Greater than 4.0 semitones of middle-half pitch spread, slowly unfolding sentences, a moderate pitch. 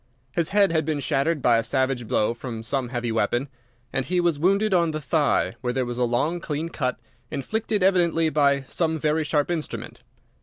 No: average, 4.9 semitones; average, 195 wpm; medium, 145 Hz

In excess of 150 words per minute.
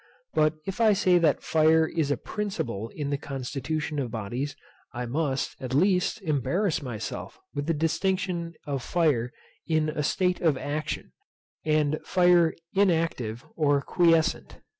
No: average, 140 wpm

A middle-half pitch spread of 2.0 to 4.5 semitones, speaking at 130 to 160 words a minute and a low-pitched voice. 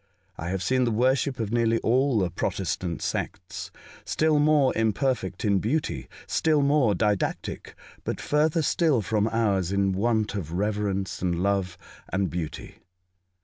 No: wide, 5.5 semitones; average, 145 wpm; low, 105 Hz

